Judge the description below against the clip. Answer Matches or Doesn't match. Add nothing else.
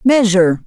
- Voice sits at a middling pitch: Doesn't match